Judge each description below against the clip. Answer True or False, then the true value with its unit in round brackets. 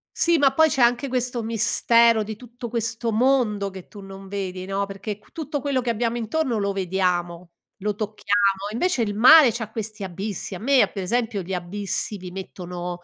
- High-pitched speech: True (215 Hz)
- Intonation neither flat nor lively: True (3.7 semitones)